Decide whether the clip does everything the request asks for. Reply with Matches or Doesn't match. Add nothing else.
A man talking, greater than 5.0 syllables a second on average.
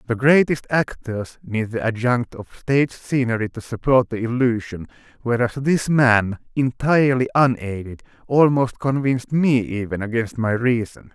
Doesn't match